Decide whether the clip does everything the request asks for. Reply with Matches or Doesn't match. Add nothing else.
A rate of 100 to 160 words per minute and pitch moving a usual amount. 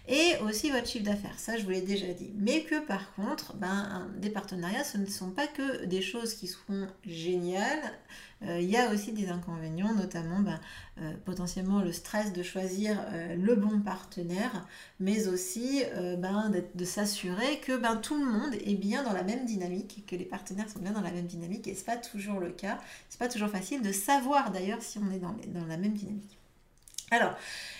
Doesn't match